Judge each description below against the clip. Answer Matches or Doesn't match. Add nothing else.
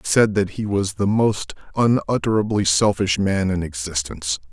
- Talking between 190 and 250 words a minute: Doesn't match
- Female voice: Doesn't match